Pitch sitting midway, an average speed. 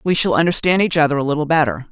No: medium, 155 Hz; fast, 250 wpm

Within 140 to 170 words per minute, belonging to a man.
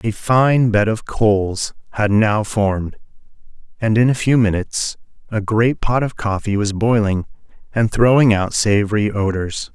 Yes: average, 155 wpm; male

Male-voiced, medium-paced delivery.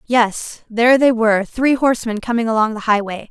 No: female; average, 180 wpm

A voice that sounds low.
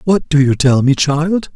No: medium, 150 Hz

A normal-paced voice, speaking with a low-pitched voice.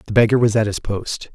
No: fast, 265 wpm; low, 110 Hz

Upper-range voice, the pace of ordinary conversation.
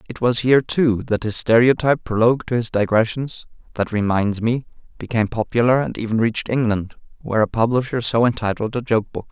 No: low, 115 Hz; average, 170 wpm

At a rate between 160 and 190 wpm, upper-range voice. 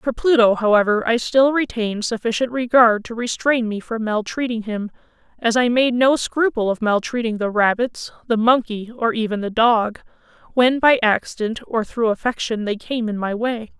Yes: average, 175 wpm; high, 230 Hz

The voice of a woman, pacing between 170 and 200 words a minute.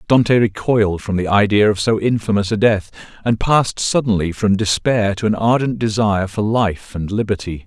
No: male; average, 180 wpm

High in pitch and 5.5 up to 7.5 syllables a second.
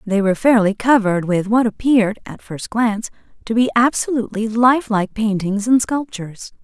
Yes: high, 220 Hz; 5.7 syllables/s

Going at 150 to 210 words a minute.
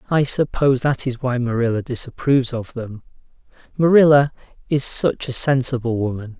No: average, 140 wpm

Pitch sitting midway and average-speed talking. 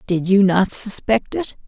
No: high, 200 Hz; average, 180 wpm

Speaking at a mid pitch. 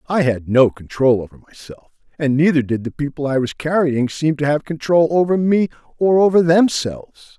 Yes: medium, 150 Hz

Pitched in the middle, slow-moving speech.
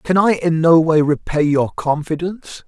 No: medium, 160 Hz; average, 180 wpm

